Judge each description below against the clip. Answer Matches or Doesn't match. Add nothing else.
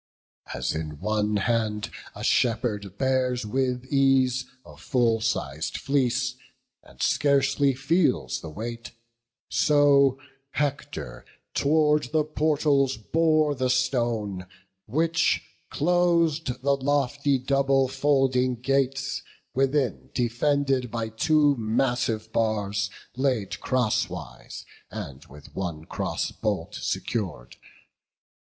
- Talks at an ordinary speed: Doesn't match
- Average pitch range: Matches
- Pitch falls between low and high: Doesn't match